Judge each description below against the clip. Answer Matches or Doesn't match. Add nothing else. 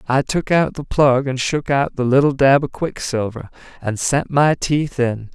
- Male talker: Matches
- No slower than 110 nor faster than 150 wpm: Doesn't match